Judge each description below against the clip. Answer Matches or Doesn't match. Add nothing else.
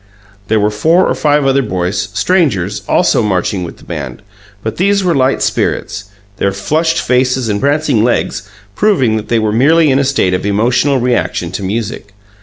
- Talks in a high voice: Doesn't match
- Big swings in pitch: Matches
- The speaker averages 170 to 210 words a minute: Matches